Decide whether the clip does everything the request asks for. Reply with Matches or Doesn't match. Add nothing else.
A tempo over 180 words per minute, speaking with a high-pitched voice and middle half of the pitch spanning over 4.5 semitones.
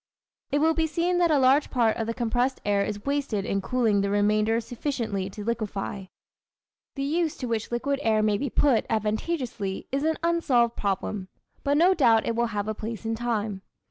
Matches